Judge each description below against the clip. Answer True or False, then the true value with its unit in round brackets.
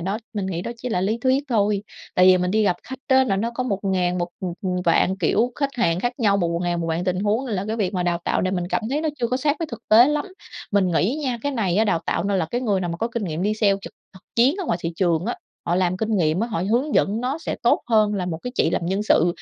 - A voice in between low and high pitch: False (200 Hz)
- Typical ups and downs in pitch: True (4.8 semitones)